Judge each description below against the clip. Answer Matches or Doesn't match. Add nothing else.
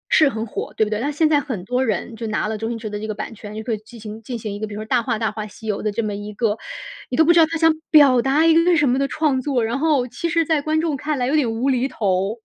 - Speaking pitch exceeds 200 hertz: Matches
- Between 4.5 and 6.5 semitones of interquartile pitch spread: Matches